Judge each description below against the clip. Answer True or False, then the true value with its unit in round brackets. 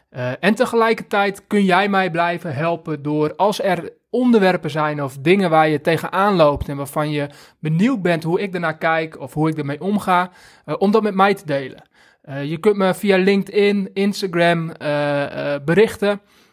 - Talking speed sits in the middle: True (180 wpm)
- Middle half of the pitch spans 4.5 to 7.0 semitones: True (4.8 semitones)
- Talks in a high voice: False (175 Hz)